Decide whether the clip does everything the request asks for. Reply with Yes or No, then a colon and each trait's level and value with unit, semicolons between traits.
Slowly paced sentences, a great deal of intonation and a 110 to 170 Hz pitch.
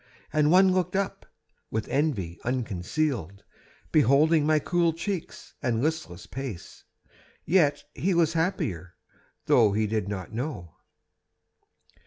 Yes: slow, 115 wpm; wide, 7.7 semitones; medium, 140 Hz